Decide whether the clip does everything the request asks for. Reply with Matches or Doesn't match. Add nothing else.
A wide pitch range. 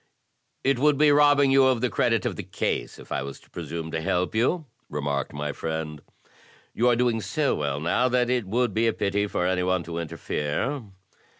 Matches